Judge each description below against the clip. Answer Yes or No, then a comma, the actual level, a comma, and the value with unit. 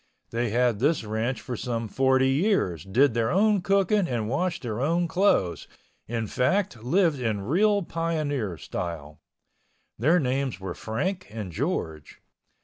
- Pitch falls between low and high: No, low, 125 Hz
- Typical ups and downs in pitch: No, wide, 7.4 semitones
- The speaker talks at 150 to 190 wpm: No, average, 140 wpm